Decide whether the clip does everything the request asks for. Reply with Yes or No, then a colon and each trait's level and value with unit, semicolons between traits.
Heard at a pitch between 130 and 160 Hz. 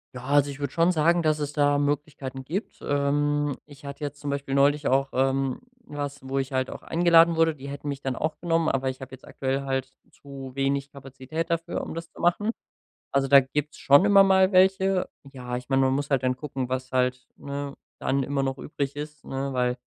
Yes: medium, 140 Hz